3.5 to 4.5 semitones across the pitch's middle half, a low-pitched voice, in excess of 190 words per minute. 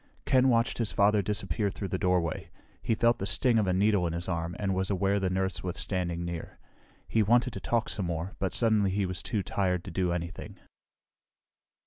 No: average, 2.9 semitones; very low, 95 Hz; fast, 205 wpm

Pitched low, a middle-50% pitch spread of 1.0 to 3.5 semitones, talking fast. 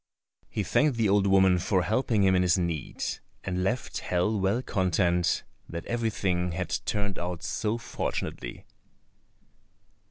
No: very low, 95 Hz; average, 3.1 semitones; slow, 135 wpm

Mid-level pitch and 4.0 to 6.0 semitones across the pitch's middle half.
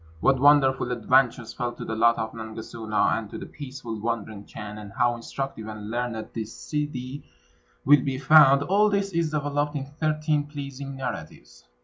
No: low, 130 Hz; average, 4.5 semitones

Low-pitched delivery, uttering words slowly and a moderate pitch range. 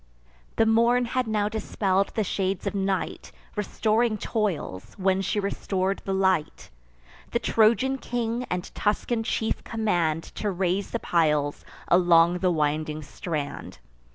No: high, 195 Hz; slow, 130 wpm; average, 4.1 semitones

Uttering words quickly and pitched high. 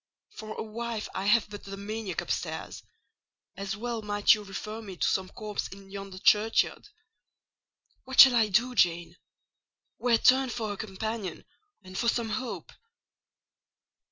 No: average, 150 wpm; high, 215 Hz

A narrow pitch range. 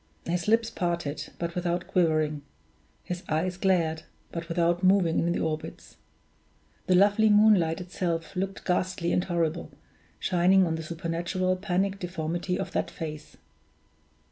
Yes: narrow, 2.1 semitones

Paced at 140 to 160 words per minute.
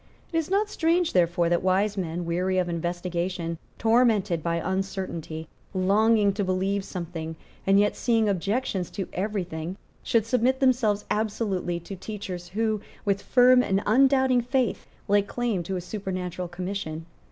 Yes: average, 150 wpm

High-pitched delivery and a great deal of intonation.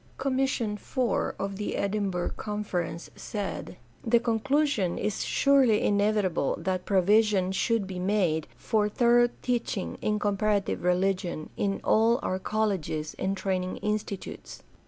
No: high, 205 Hz; average, 2.9 semitones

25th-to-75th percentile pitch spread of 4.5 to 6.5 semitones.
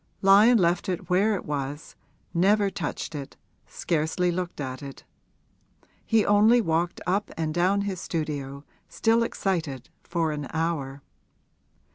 Yes: average, 4.8 semitones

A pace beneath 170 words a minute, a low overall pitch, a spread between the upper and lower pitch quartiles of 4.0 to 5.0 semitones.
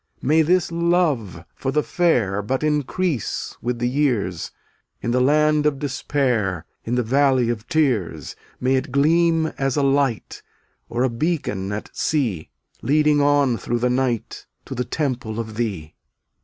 Yes: average, 155 wpm; low, 130 Hz; average, 4.4 semitones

